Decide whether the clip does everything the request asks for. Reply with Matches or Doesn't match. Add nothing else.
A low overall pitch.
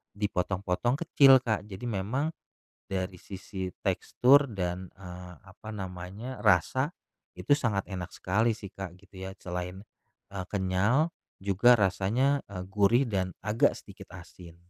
Matches